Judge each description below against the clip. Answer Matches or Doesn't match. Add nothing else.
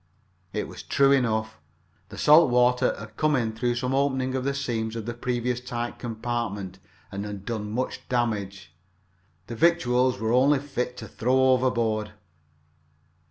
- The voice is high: Doesn't match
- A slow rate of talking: Doesn't match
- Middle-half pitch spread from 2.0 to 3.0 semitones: Matches